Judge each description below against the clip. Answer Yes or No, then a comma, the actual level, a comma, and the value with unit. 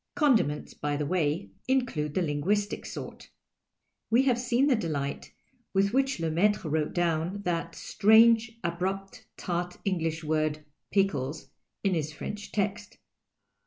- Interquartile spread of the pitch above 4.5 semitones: Yes, average, 5.2 semitones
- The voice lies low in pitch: No, medium, 180 Hz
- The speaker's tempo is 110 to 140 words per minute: Yes, slow, 135 wpm